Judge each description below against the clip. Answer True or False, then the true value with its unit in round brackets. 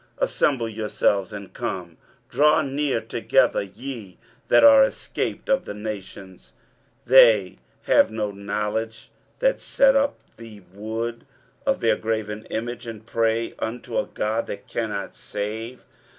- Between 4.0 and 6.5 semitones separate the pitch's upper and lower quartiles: False (2.7 semitones)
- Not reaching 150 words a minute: True (135 wpm)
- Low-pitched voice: True (110 Hz)